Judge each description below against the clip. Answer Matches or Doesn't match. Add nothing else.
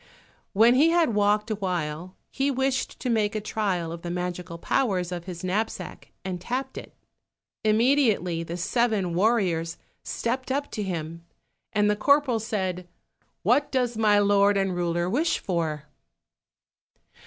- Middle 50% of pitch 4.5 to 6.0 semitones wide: Matches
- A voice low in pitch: Doesn't match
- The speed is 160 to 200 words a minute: Doesn't match